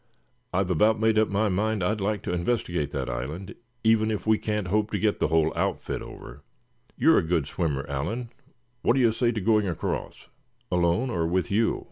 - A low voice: Yes, low, 100 Hz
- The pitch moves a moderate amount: Yes, average, 4.4 semitones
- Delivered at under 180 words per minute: No, average, 195 wpm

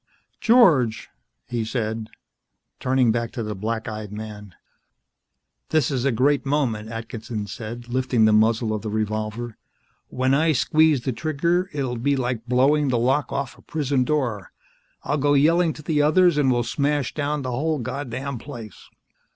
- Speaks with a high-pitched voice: No, low, 125 Hz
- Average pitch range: Yes, average, 4.5 semitones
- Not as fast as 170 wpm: Yes, average, 160 wpm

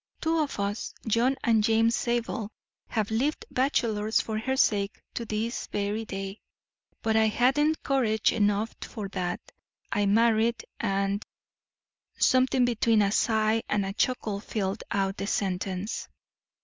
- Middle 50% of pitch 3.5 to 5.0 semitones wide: No, narrow, 2.6 semitones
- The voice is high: Yes, high, 220 Hz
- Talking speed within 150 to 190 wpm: No, slow, 135 wpm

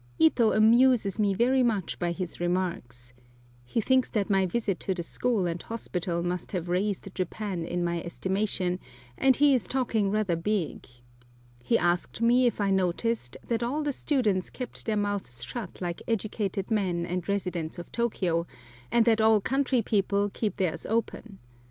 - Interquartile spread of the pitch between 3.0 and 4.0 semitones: No, average, 4.5 semitones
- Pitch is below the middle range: No, high, 200 Hz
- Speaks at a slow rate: No, average, 165 wpm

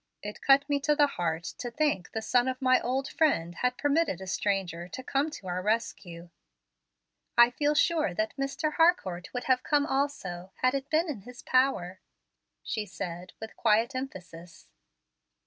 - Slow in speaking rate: No, average, 170 wpm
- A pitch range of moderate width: No, wide, 7.3 semitones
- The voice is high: Yes, high, 245 Hz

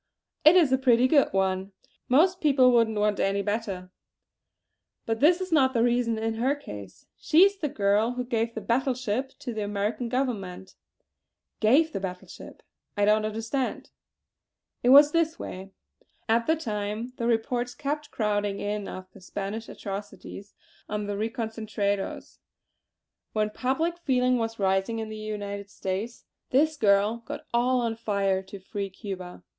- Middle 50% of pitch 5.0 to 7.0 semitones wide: No, average, 4.0 semitones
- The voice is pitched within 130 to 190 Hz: No, high, 225 Hz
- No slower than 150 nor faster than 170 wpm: Yes, average, 160 wpm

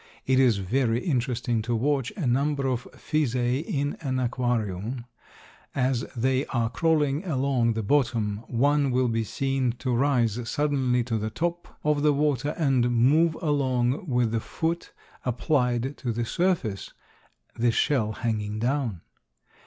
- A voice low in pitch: Yes, low, 125 Hz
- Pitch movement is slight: No, average, 3.5 semitones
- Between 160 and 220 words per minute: No, average, 145 wpm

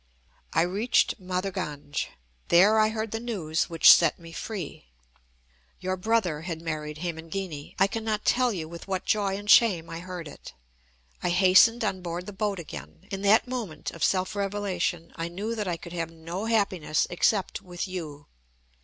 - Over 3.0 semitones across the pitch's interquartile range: Yes, average, 3.7 semitones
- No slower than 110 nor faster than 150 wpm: No, average, 170 wpm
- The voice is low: No, medium, 185 Hz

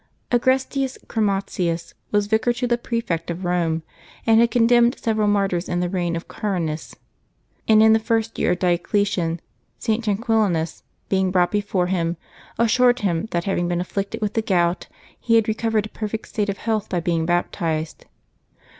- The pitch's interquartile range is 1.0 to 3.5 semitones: No, average, 4.3 semitones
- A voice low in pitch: No, high, 200 Hz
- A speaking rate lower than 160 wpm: No, average, 165 wpm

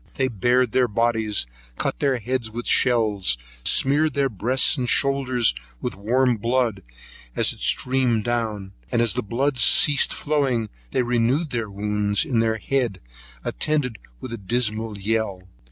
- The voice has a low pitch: Yes, low, 120 Hz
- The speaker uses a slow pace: No, average, 155 wpm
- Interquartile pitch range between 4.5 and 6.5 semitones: No, average, 3.3 semitones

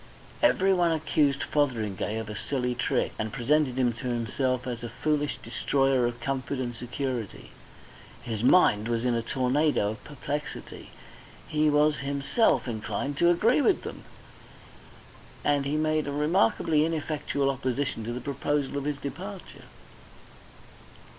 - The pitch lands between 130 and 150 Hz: Yes, medium, 140 Hz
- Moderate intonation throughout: Yes, average, 3.7 semitones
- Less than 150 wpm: Yes, average, 140 wpm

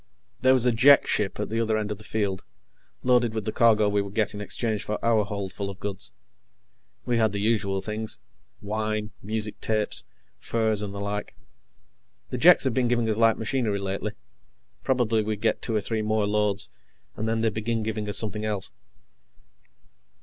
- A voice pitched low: Yes, low, 110 Hz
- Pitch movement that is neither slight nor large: No, narrow, 1.7 semitones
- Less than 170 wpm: No, average, 185 wpm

